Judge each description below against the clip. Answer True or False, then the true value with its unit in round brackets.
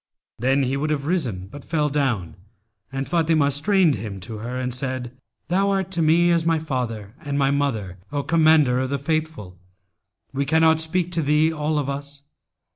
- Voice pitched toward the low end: False (145 Hz)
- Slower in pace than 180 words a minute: False (185 wpm)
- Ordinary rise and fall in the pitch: True (3.9 semitones)